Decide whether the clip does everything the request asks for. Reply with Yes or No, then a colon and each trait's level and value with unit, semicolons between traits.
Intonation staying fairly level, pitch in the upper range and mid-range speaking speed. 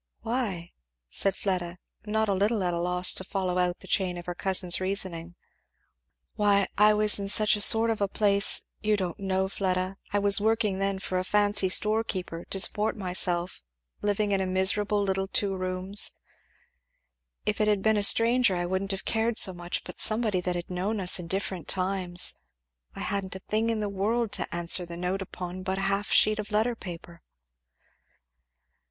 Yes: narrow, 2.3 semitones; high, 195 Hz; average, 190 wpm